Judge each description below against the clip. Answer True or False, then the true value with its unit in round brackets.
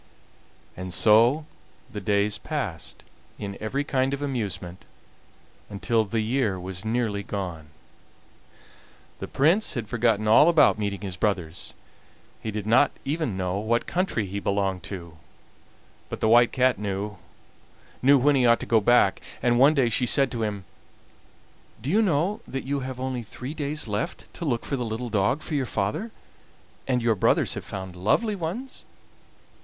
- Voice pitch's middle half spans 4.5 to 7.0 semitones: True (5.2 semitones)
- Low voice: True (115 Hz)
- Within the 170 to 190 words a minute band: False (160 wpm)